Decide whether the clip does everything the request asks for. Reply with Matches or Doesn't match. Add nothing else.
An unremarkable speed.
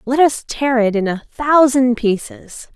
Matches